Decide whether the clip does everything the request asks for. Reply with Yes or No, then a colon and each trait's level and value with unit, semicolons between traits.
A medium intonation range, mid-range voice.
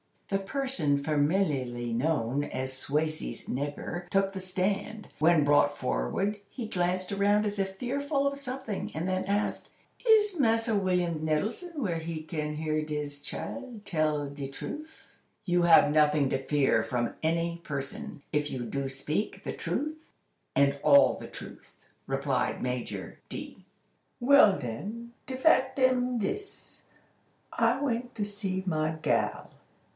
No: wide, 7.5 semitones; medium, 175 Hz